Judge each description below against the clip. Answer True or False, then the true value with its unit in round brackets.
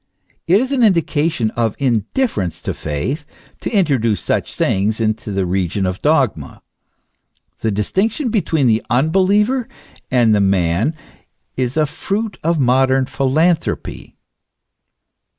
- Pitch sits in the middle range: False (130 Hz)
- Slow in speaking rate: True (120 wpm)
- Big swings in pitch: True (8.1 semitones)